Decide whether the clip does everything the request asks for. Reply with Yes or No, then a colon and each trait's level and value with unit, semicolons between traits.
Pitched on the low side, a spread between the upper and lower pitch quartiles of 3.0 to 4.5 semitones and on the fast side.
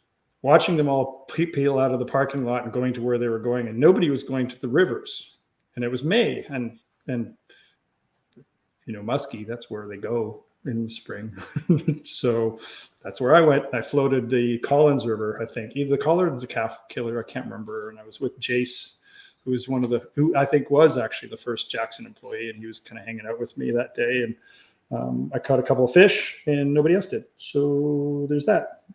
Yes: low, 125 Hz; average, 3.7 semitones; fast, 220 wpm